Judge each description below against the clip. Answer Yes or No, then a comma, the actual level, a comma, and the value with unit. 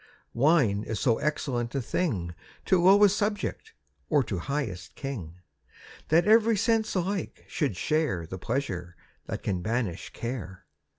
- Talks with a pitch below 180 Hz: Yes, low, 135 Hz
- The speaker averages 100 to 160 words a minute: Yes, slow, 135 wpm